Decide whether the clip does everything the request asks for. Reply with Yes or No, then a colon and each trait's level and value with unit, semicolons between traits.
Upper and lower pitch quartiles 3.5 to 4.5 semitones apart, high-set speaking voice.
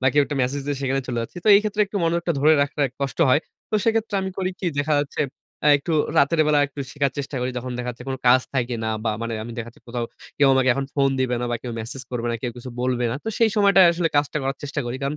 No: average, 4.0 semitones; medium, 140 Hz